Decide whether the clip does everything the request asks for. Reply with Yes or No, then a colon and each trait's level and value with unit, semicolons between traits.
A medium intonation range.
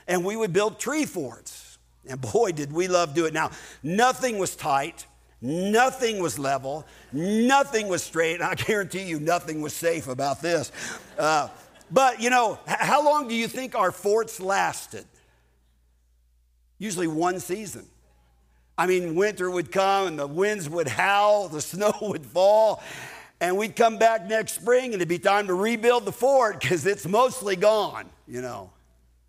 No: wide, 6.6 semitones